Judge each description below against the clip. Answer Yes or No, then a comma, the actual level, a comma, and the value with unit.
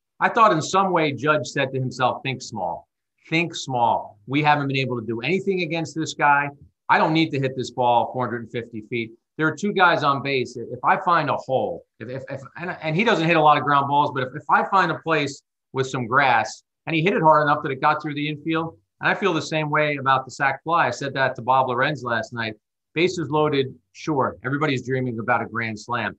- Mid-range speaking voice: Yes, medium, 145 Hz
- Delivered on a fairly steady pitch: No, average, 4.0 semitones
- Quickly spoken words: Yes, fast, 245 wpm